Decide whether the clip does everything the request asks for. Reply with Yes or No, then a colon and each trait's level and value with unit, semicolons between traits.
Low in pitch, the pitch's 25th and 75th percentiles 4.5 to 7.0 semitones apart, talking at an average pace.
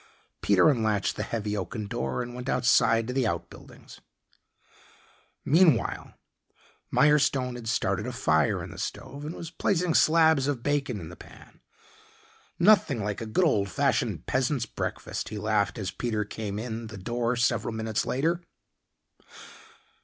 Yes: low, 120 Hz; average, 4.8 semitones; average, 145 wpm